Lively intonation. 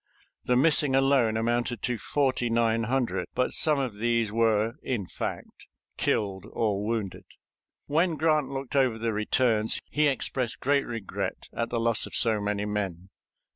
No: average, 3.7 semitones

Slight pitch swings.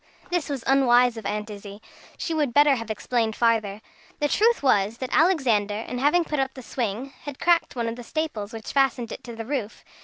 No: average, 4.4 semitones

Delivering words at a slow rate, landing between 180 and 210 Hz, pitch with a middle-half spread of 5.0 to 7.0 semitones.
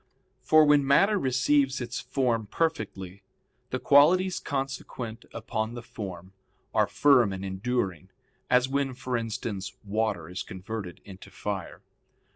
No: slow, 125 wpm; low, 115 Hz; wide, 5.6 semitones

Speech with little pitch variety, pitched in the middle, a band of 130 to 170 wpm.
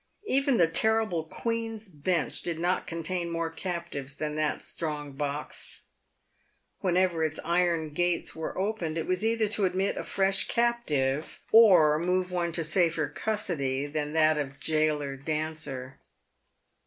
No: average, 3.5 semitones; medium, 165 Hz; average, 140 wpm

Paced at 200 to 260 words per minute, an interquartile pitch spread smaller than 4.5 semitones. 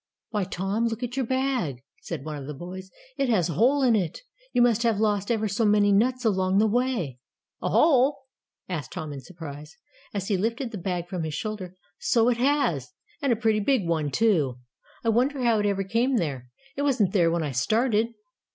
No: fast, 205 wpm; wide, 5.5 semitones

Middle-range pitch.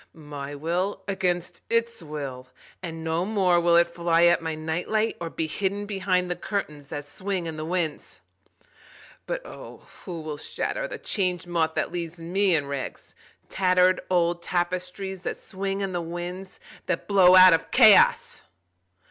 Yes: medium, 175 Hz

